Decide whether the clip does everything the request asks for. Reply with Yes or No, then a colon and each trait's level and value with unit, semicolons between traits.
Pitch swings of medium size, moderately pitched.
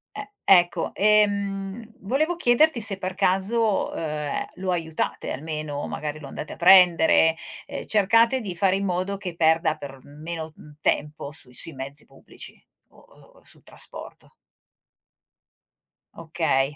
Yes: average, 4.5 semitones; medium, 175 Hz